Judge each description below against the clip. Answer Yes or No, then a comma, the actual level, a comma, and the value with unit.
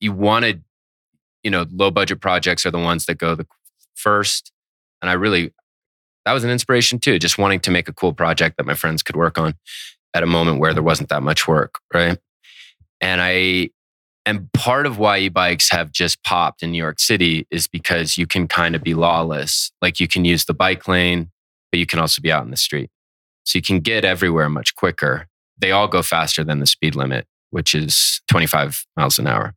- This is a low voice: Yes, very low, 85 Hz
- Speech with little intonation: Yes, narrow, 2.3 semitones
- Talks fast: Yes, fast, 215 wpm